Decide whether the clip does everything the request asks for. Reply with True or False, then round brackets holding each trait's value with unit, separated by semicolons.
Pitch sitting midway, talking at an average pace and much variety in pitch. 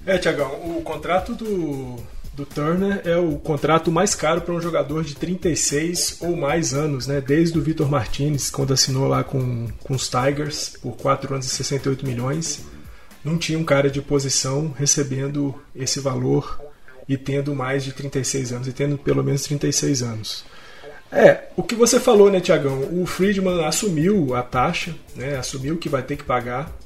False (145 Hz; 170 wpm; 3.3 semitones)